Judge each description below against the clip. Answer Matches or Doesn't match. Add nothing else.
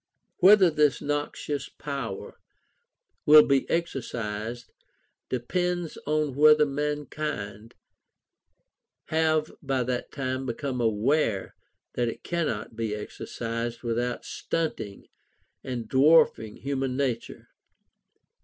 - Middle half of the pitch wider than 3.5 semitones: Matches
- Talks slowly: Matches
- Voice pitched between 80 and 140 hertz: Matches